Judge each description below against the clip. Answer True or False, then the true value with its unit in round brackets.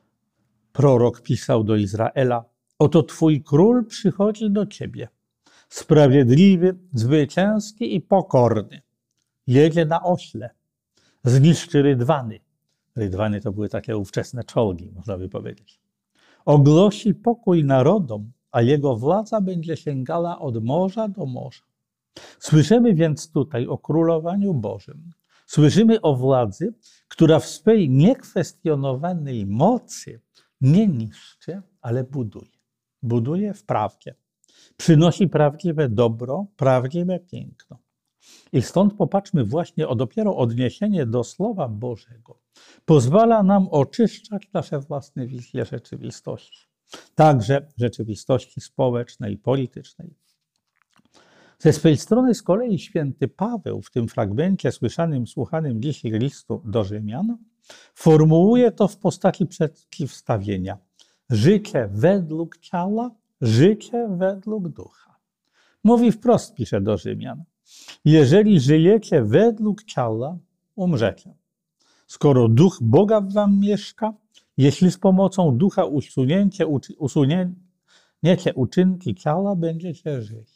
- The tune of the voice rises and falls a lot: True (7.3 semitones)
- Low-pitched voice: False (155 Hz)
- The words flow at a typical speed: False (105 wpm)